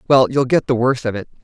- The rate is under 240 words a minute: No, fast, 250 wpm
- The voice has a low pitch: Yes, low, 125 Hz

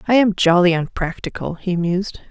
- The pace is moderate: Yes, average, 155 wpm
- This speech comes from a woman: Yes, female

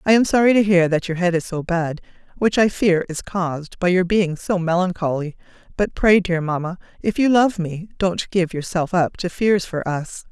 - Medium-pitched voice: Yes, medium, 180 Hz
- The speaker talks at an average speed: No, fast, 215 wpm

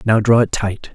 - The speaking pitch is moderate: No, low, 110 Hz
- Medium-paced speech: No, fast, 255 wpm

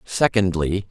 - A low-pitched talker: Yes, very low, 95 Hz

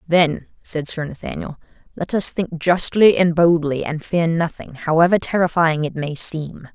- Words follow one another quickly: No, average, 160 wpm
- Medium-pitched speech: Yes, medium, 165 Hz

